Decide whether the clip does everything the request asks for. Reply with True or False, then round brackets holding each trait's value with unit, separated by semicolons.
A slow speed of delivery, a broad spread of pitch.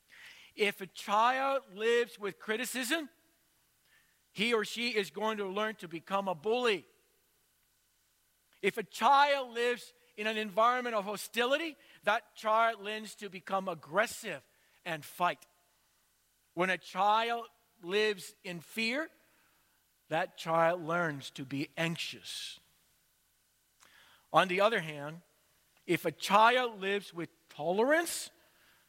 False (115 wpm; 4.9 semitones)